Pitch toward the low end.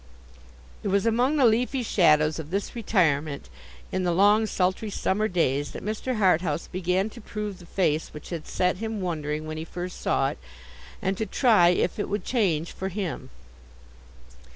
No: medium, 185 Hz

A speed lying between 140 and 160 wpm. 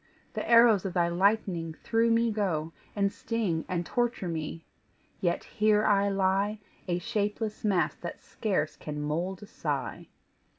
Yes: average, 145 wpm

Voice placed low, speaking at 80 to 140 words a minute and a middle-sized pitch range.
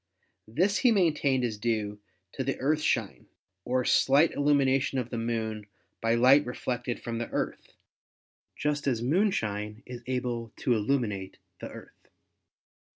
Yes: low, 125 Hz; slow, 135 wpm; average, 3.6 semitones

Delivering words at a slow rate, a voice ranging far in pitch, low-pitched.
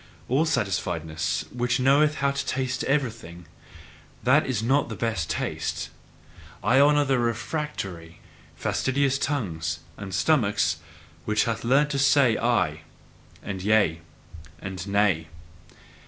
Yes: slow, 120 wpm; wide, 6.6 semitones; low, 115 Hz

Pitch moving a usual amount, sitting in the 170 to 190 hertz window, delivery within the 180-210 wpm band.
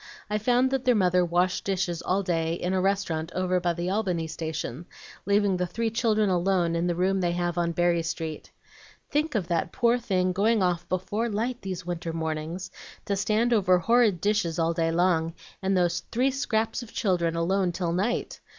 Yes: average, 3.6 semitones; medium, 185 Hz; average, 190 wpm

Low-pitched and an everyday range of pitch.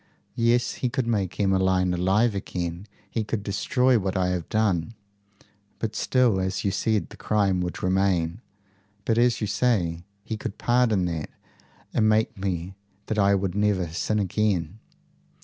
Yes: low, 100 Hz; average, 3.1 semitones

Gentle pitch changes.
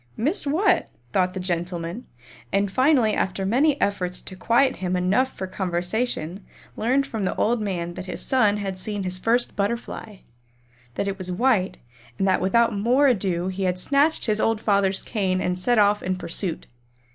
No: average, 4.3 semitones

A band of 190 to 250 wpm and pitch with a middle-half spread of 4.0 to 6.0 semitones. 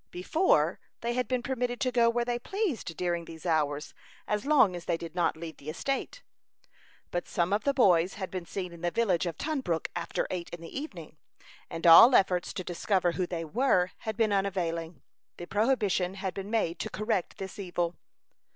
Yes: average, 195 wpm; wide, 5.4 semitones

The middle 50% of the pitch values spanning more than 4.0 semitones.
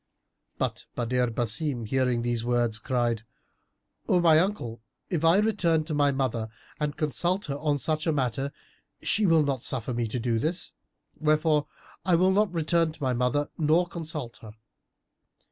Yes: average, 5.2 semitones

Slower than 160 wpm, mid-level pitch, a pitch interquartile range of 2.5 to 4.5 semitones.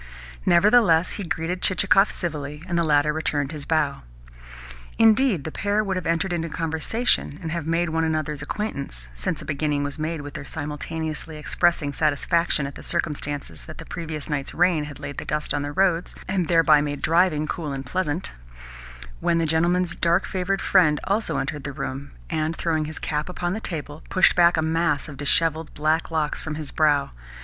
No: average, 185 wpm; medium, 160 Hz; average, 2.8 semitones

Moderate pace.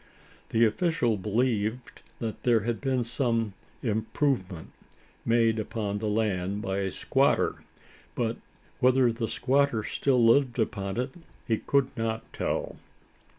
No: slow, 120 wpm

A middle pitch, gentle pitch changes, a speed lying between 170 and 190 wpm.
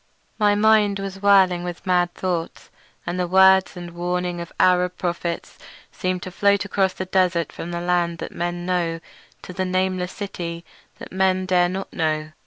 Yes: medium, 180 Hz; narrow, 1.5 semitones; average, 175 wpm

